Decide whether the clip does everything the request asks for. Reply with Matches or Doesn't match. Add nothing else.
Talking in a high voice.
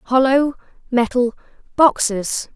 Matches